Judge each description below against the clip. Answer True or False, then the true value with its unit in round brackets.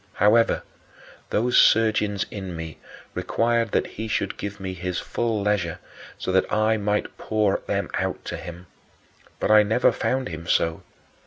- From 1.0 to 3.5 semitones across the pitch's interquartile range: True (3.1 semitones)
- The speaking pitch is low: True (105 Hz)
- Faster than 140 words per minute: True (155 wpm)